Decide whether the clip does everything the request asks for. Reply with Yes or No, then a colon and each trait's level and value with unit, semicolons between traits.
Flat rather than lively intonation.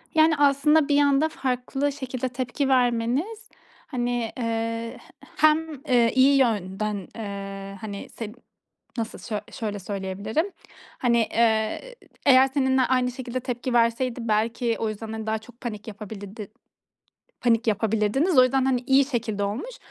No: average, 3.6 semitones